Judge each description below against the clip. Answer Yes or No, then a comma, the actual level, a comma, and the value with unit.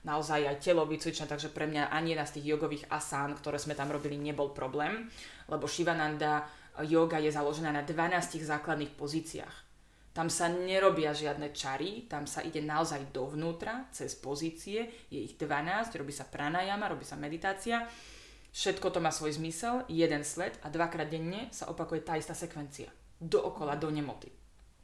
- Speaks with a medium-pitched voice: Yes, medium, 155 Hz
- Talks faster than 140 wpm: Yes, average, 160 wpm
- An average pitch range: No, narrow, 2.3 semitones